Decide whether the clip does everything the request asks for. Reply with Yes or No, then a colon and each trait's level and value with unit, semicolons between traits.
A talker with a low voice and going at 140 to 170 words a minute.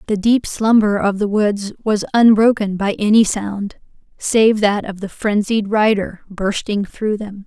No: high, 210 Hz; average, 160 wpm